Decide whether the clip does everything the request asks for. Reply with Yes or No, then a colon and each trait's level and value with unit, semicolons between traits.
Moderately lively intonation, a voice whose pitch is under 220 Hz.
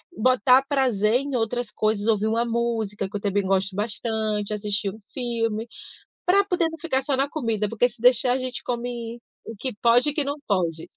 No: average, 3.4 semitones; high, 230 Hz